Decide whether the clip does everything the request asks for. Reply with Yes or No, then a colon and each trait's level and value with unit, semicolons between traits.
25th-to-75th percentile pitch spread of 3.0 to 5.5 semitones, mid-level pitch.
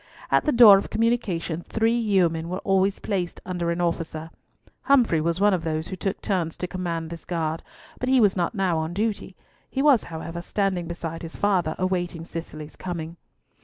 Yes: average, 3.3 semitones; medium, 175 Hz